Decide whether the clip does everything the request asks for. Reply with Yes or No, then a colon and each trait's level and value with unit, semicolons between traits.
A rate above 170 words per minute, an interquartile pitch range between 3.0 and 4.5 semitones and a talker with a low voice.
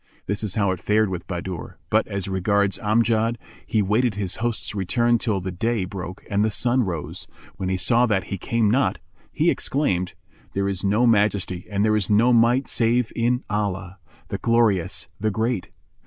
Yes: average, 185 wpm; average, 3.3 semitones; low, 105 Hz